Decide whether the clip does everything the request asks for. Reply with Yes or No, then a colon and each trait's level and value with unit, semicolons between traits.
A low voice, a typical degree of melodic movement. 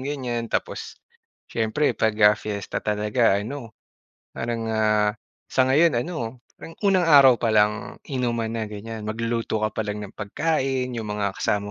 Yes: low, 115 Hz; average, 3.5 semitones